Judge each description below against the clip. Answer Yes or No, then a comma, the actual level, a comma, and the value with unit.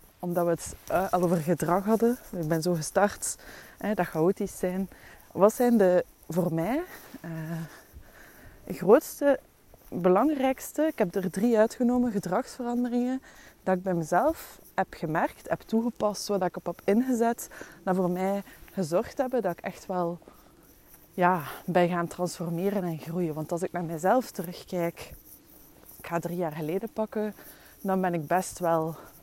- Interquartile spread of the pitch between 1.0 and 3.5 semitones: No, average, 4.0 semitones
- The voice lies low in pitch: No, medium, 185 Hz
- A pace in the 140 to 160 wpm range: Yes, average, 150 wpm